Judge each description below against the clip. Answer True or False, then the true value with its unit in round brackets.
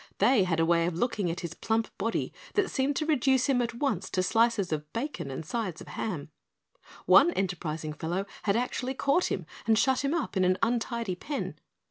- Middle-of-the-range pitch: False (220 Hz)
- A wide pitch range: True (6.6 semitones)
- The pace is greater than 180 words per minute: True (200 wpm)